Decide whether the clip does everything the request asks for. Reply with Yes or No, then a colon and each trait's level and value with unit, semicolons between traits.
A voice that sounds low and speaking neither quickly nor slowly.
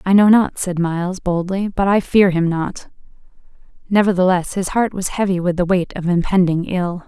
No: medium, 185 Hz; average, 185 wpm